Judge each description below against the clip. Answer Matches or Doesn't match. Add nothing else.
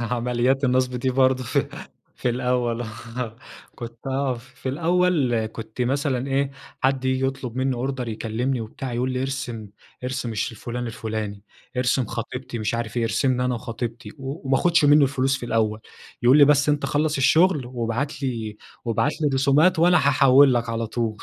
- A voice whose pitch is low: Matches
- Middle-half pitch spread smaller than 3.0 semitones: Matches